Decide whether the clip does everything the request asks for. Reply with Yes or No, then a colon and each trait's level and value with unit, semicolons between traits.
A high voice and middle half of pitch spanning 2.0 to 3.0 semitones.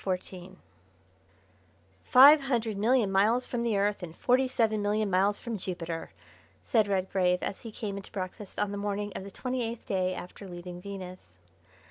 No: high, 200 Hz; average, 3.4 semitones